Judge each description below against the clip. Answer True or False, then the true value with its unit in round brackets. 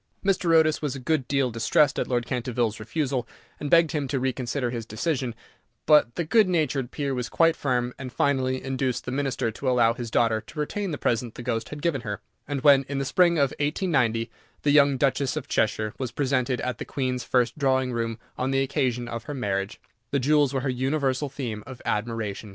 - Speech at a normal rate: False (210 wpm)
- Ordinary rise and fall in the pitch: True (3.1 semitones)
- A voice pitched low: True (130 Hz)